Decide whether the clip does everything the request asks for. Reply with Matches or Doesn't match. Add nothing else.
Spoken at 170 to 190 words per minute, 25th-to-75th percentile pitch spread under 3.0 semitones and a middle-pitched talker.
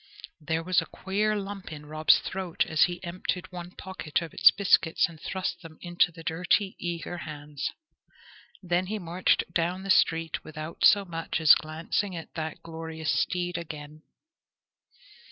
Doesn't match